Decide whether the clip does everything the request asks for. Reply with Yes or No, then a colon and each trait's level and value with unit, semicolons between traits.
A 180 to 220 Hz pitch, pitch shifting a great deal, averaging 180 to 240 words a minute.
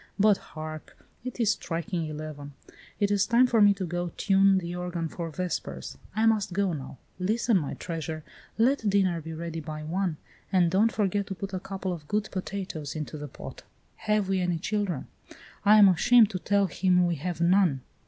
No: medium, 185 Hz; average, 3.8 semitones; average, 190 wpm